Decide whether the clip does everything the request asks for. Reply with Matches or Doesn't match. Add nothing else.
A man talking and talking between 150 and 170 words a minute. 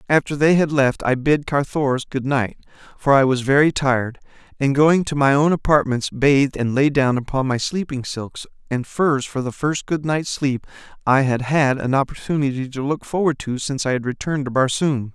Doesn't match